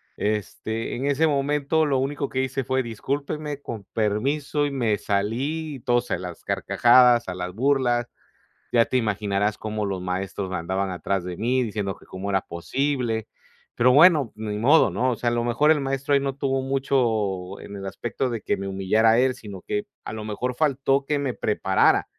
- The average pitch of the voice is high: No, low, 120 Hz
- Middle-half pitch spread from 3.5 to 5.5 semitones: Yes, average, 5.0 semitones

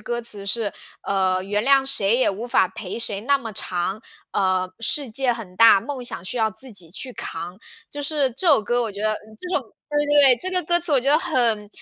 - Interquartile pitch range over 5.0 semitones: Yes, wide, 5.4 semitones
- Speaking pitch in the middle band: No, high, 230 Hz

